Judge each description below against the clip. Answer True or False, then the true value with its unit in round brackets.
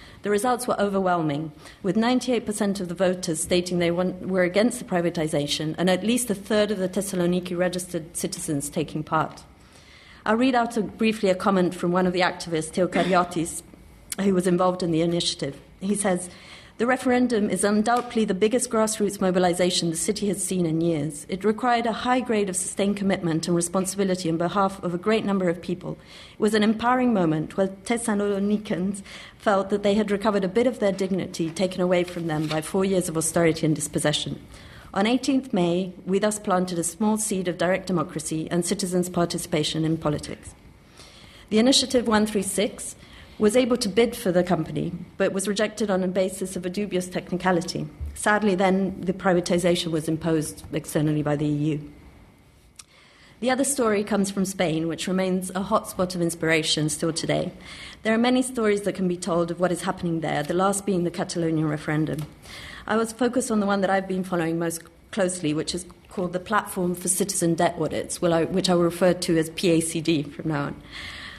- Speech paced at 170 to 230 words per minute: True (185 wpm)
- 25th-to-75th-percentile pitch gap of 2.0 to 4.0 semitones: True (3.3 semitones)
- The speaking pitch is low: False (185 Hz)